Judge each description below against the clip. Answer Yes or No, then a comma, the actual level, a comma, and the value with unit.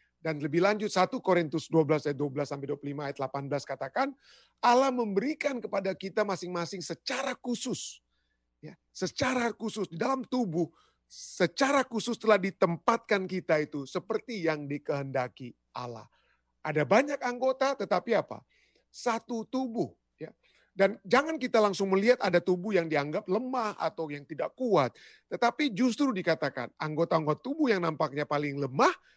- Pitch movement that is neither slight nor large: No, wide, 7.8 semitones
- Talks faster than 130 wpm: Yes, fast, 140 wpm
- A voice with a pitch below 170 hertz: No, high, 190 Hz